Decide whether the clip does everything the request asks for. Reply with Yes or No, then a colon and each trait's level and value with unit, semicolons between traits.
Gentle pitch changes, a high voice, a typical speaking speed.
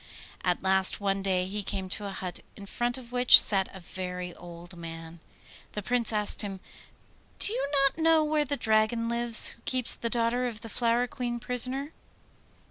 No: average, 4.5 semitones; high, 225 Hz; average, 185 wpm